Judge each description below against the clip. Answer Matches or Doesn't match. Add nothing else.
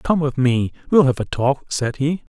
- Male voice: Matches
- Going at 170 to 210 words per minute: Doesn't match